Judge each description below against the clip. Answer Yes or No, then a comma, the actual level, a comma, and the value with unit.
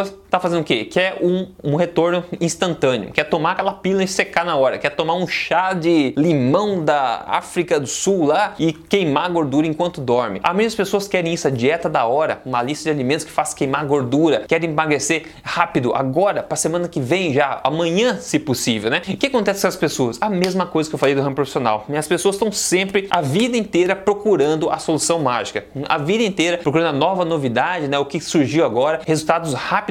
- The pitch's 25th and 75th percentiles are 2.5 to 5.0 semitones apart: Yes, average, 4.0 semitones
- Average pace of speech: No, fast, 205 wpm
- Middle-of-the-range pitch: Yes, medium, 165 Hz